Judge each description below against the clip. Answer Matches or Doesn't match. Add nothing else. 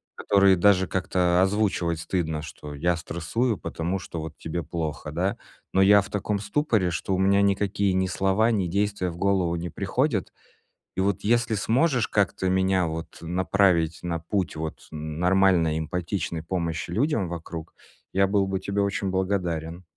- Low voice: Matches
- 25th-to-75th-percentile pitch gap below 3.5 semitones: Matches